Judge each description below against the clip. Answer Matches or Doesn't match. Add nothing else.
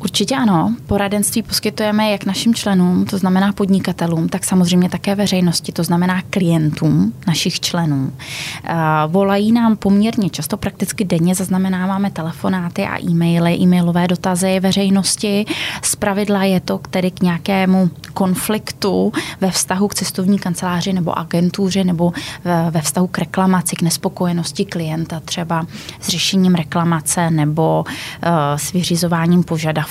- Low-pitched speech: Doesn't match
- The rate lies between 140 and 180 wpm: Doesn't match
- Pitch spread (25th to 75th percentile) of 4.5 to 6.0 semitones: Doesn't match